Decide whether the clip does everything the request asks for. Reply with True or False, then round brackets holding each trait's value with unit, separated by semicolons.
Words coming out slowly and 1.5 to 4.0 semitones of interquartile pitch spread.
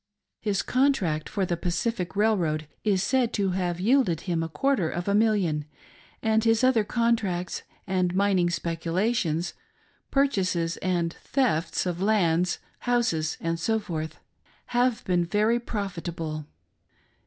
False (120 wpm; 4.7 semitones)